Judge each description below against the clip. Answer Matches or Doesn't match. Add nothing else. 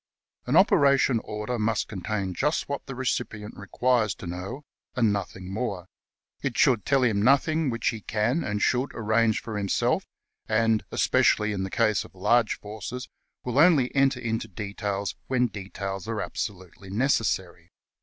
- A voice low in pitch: Matches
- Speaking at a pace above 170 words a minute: Doesn't match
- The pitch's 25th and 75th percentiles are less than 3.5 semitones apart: Doesn't match